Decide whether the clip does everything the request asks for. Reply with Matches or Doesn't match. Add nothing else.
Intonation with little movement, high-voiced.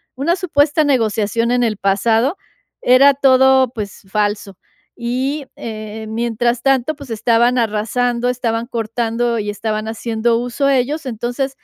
Doesn't match